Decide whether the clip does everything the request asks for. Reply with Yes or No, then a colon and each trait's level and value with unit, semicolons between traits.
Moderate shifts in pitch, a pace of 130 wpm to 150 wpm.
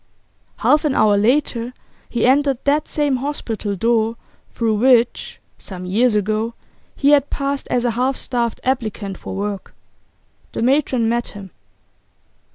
Yes: average, 3.9 semitones; average, 140 wpm